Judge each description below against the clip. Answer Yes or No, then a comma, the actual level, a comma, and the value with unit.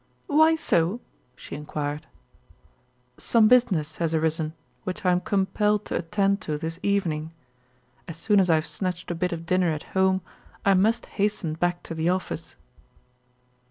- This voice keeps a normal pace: Yes, average, 160 wpm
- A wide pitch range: No, average, 3.7 semitones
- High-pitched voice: No, medium, 180 Hz